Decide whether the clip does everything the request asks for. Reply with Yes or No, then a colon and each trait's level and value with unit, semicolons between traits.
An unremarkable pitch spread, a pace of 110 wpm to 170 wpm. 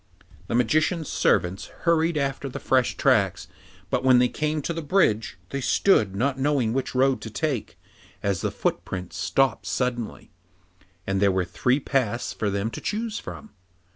No: wide, 5.8 semitones; average, 165 wpm